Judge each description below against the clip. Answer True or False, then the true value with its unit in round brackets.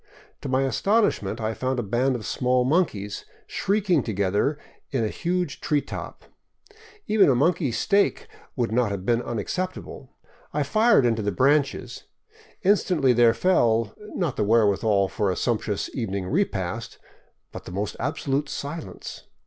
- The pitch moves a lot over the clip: True (5.9 semitones)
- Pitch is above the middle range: False (125 Hz)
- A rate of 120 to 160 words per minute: True (145 wpm)